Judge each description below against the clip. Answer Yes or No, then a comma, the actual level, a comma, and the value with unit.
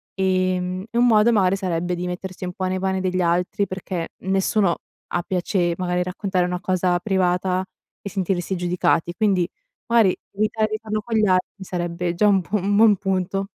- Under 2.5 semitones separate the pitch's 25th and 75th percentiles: Yes, narrow, 1.8 semitones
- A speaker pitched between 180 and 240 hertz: Yes, medium, 185 Hz